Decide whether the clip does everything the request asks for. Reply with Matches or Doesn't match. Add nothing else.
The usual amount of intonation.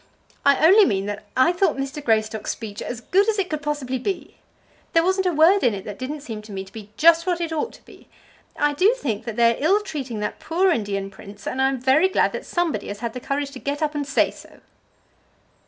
Doesn't match